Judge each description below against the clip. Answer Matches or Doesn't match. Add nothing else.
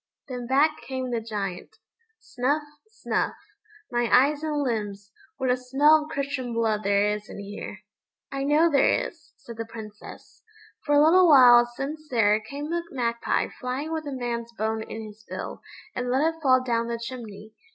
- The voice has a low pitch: Doesn't match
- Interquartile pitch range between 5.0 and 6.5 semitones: Doesn't match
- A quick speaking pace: Doesn't match